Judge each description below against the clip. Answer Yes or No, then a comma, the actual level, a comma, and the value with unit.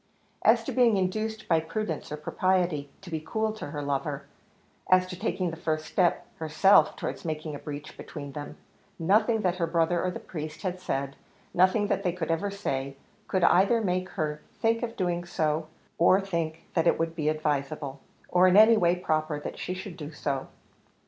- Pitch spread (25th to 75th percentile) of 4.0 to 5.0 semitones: No, average, 3.4 semitones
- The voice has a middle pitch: Yes, medium, 170 Hz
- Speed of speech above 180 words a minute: Yes, average, 190 wpm